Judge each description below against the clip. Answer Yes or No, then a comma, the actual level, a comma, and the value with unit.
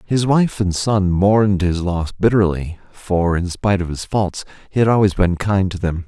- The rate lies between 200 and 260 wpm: Yes, fast, 205 wpm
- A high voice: No, very low, 95 Hz